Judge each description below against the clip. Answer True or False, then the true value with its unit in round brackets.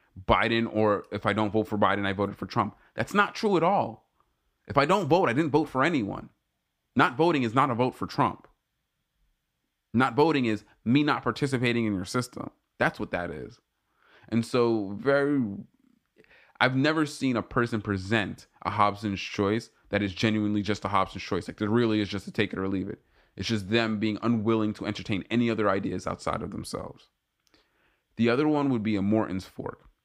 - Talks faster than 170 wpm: True (195 wpm)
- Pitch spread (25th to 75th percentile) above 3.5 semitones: False (3.2 semitones)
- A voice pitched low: True (110 Hz)